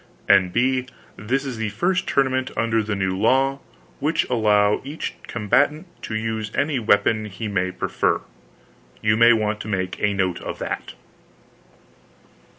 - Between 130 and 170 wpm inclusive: Yes, average, 150 wpm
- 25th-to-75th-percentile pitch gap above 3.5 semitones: Yes, average, 4.1 semitones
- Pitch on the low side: Yes, low, 110 Hz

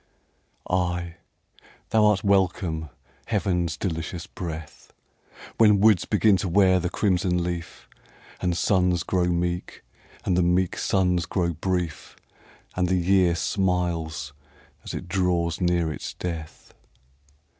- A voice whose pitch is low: Yes, very low, 90 Hz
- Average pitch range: No, narrow, 1.6 semitones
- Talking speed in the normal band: No, slow, 120 wpm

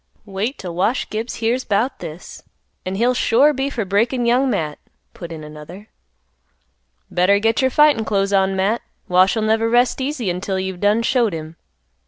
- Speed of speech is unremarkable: Yes, average, 170 wpm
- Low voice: No, high, 215 Hz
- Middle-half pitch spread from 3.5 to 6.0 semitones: Yes, average, 4.4 semitones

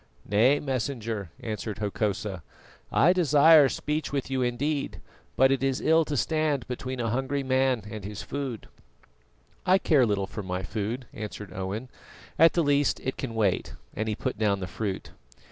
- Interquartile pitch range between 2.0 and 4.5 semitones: No, average, 5.1 semitones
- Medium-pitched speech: No, low, 125 Hz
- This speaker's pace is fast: No, average, 165 wpm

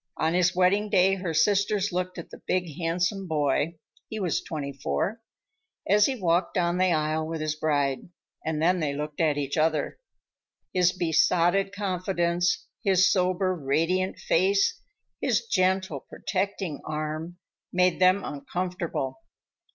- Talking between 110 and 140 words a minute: Yes, slow, 135 wpm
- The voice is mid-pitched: Yes, medium, 175 Hz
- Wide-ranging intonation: No, average, 3.2 semitones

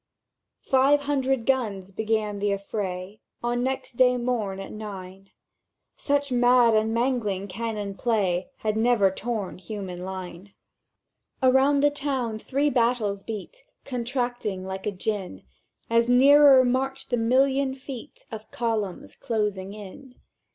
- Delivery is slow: Yes, slow, 125 wpm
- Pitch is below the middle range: No, high, 230 Hz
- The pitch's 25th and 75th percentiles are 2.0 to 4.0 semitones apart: No, average, 4.5 semitones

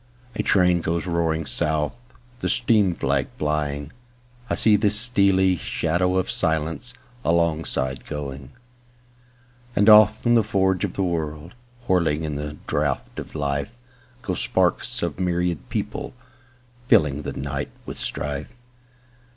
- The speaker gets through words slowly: Yes, slow, 105 wpm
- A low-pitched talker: Yes, very low, 90 Hz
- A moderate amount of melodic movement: No, wide, 8.0 semitones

